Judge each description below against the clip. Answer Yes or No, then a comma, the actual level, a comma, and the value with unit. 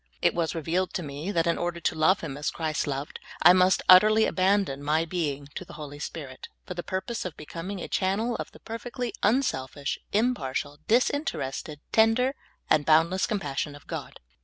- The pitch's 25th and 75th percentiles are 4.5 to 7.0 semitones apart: Yes, wide, 5.5 semitones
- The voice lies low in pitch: No, medium, 170 Hz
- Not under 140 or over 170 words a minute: No, average, 185 wpm